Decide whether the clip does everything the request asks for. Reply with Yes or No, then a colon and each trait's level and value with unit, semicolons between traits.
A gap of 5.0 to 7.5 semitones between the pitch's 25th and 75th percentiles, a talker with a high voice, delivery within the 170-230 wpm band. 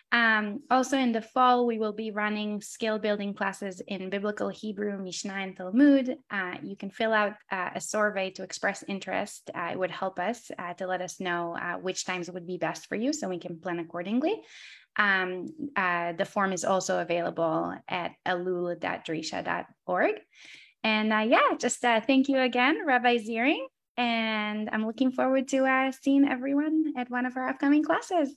Yes: average, 5.3 semitones; high, 215 Hz; average, 180 wpm